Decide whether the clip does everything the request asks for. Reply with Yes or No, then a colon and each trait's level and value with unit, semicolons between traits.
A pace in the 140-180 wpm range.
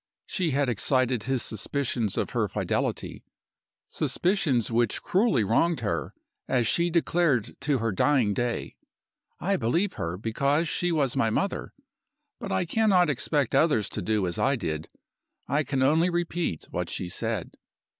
Yes: average, 150 wpm